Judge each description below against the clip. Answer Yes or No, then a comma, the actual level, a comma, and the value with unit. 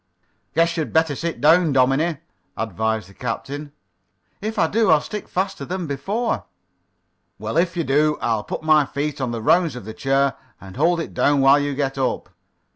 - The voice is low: No, medium, 145 Hz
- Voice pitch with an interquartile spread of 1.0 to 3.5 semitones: No, average, 4.0 semitones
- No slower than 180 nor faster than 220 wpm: Yes, average, 185 wpm